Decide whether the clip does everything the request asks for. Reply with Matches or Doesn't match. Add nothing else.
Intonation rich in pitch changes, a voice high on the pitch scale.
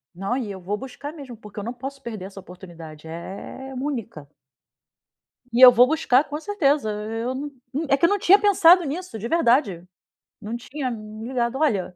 Matches